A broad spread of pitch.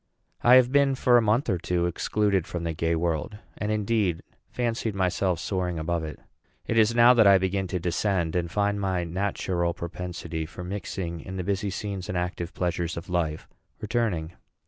No: average, 3.4 semitones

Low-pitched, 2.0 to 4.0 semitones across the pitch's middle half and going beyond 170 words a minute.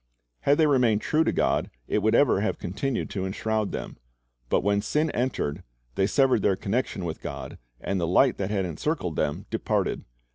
No: low, 105 Hz; wide, 5.6 semitones; average, 185 wpm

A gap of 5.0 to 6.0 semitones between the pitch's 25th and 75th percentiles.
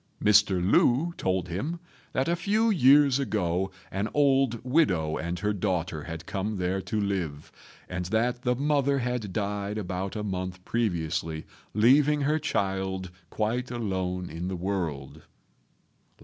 Yes: wide, 5.6 semitones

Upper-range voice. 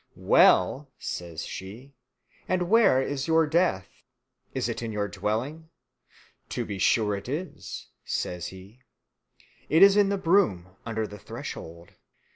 No: low, 120 Hz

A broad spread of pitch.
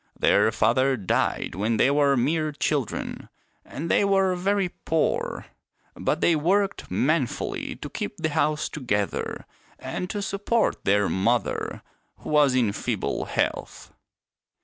Yes: wide, 6.8 semitones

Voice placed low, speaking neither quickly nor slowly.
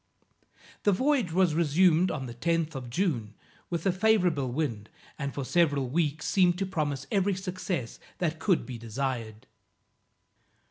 No: medium, 160 Hz; average, 145 wpm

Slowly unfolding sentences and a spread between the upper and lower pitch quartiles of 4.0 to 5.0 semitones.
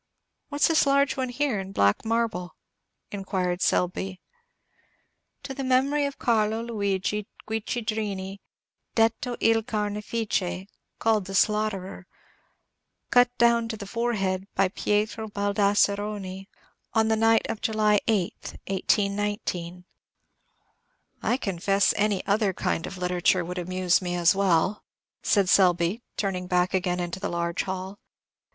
No: slow, 125 wpm; average, 3.2 semitones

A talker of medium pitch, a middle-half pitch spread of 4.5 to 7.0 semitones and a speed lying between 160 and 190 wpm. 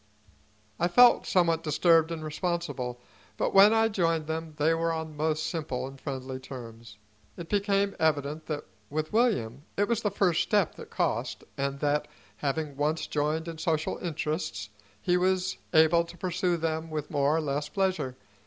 No: medium, 160 Hz; average, 3.4 semitones; average, 165 wpm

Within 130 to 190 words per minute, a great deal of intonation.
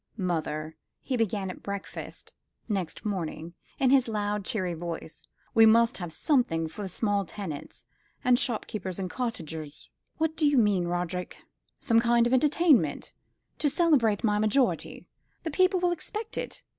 Yes: average, 150 wpm; wide, 6.2 semitones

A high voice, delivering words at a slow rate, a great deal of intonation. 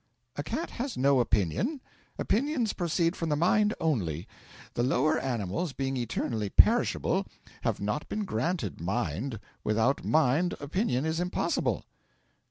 No: medium, 140 Hz; slow, 130 wpm; wide, 7.7 semitones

